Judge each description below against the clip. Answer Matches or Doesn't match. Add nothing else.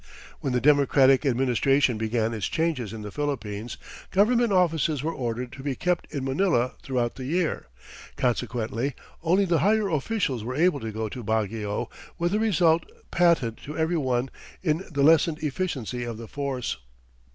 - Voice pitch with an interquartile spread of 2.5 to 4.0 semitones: Doesn't match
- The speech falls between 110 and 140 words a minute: Doesn't match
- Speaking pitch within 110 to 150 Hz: Matches